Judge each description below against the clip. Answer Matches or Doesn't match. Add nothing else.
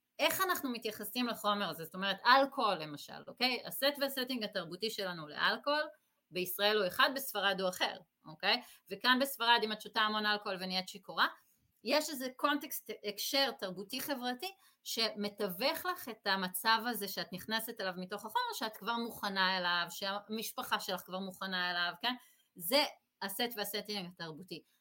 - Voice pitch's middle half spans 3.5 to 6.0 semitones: Matches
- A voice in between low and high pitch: Doesn't match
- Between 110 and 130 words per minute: Doesn't match